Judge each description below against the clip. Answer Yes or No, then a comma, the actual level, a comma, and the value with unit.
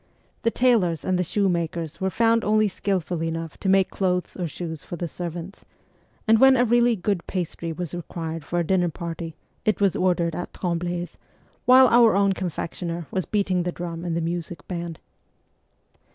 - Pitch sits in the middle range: Yes, medium, 175 Hz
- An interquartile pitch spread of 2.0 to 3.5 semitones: Yes, average, 2.9 semitones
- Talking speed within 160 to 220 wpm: Yes, average, 180 wpm